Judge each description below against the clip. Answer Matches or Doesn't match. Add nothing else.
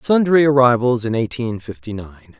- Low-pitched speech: Matches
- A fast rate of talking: Doesn't match